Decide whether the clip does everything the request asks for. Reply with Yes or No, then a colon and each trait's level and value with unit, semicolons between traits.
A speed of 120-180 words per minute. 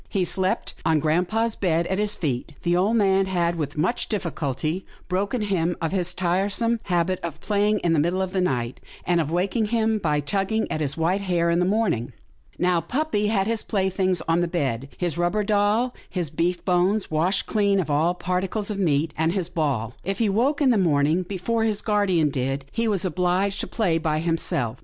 No: fast, 205 wpm